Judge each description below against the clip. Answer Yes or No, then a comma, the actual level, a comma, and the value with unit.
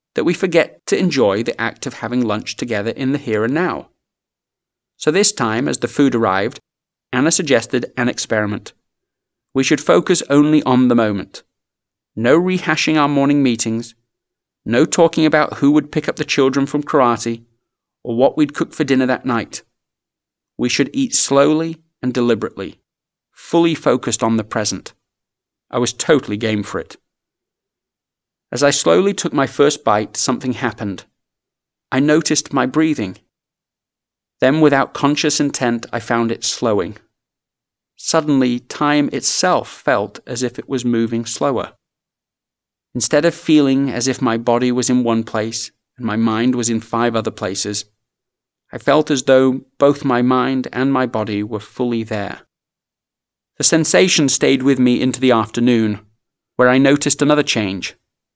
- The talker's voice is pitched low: Yes, low, 130 Hz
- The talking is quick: No, average, 155 wpm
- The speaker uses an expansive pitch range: No, average, 4.2 semitones